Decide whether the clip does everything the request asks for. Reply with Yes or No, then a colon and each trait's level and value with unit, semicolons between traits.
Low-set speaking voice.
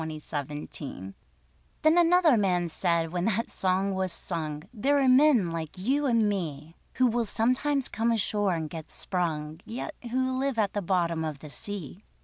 No: high, 190 Hz